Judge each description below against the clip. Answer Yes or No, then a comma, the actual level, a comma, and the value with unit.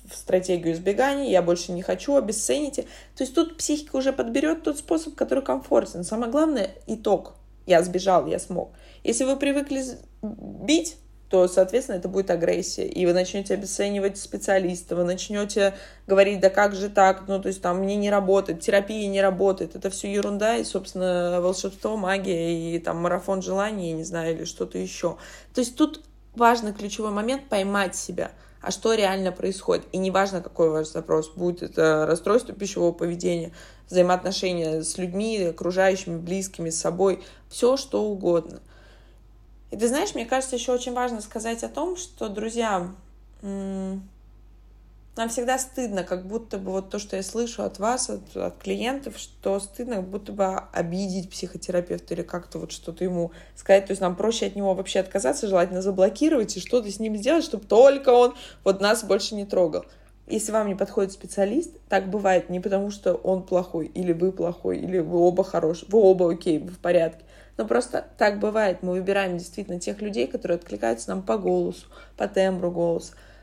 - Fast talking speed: Yes, fast, 175 wpm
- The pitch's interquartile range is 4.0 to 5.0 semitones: No, average, 3.6 semitones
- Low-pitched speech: No, high, 195 Hz